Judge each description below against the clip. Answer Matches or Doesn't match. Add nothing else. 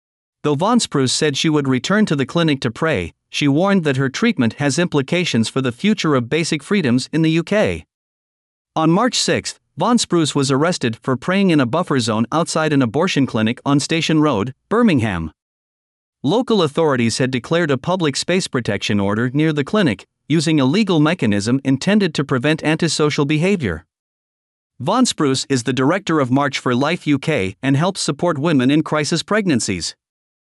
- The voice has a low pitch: Doesn't match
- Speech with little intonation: Doesn't match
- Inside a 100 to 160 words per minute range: Doesn't match